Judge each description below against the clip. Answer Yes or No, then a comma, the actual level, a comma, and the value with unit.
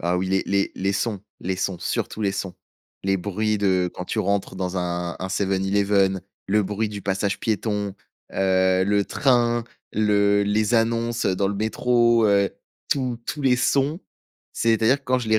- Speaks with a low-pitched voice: Yes, low, 100 Hz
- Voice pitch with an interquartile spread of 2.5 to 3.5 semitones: Yes, average, 2.9 semitones